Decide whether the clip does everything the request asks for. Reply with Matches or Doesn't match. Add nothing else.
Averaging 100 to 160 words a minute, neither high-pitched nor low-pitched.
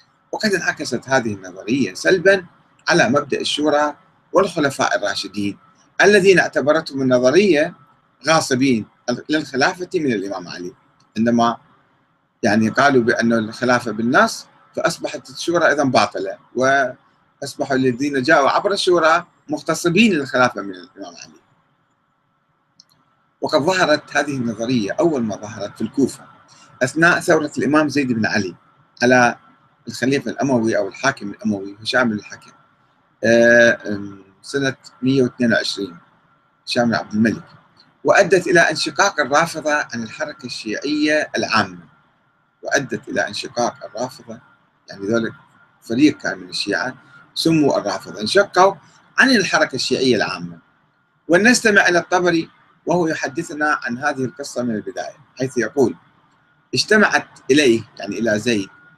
Doesn't match